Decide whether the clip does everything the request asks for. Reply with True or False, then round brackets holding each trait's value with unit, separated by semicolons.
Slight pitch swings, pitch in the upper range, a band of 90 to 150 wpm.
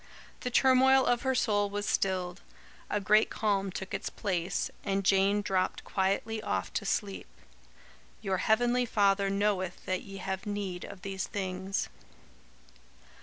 True (1.9 semitones; 195 Hz; 140 wpm)